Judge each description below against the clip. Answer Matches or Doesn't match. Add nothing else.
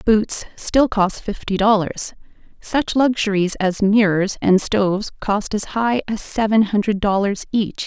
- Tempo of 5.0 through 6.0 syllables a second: Doesn't match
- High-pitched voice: Matches